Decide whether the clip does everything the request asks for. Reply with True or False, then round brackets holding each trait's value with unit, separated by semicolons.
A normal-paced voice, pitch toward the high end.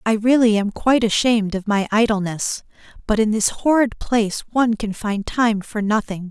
True (180 wpm; 220 Hz)